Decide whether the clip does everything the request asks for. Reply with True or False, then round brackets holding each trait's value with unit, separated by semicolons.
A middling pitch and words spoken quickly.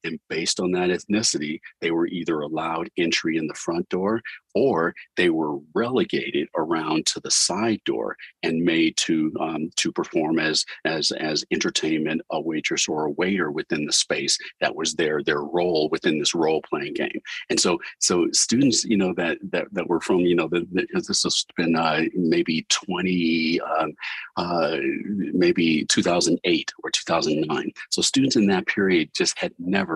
False (175 Hz; 180 wpm)